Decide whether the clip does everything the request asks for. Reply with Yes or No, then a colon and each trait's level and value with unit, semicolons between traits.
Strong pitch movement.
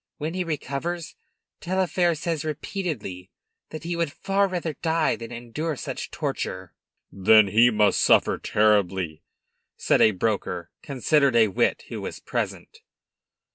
Yes: wide, 7.8 semitones